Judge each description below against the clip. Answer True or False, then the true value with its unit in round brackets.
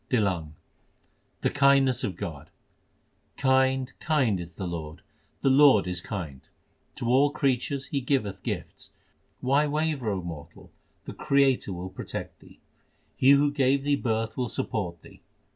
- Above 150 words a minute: False (145 wpm)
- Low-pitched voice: True (125 Hz)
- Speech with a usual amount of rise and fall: False (7.3 semitones)